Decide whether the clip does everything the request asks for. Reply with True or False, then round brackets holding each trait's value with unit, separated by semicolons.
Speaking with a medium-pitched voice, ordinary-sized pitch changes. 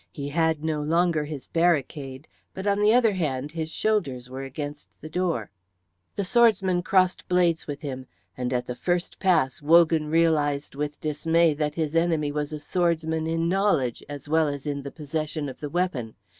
True (155 Hz; 3.0 semitones)